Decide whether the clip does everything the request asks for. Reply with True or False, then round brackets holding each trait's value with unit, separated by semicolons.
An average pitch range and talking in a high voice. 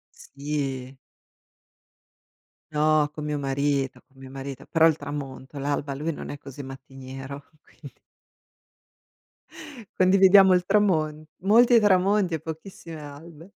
False (4.0 semitones; 150 Hz)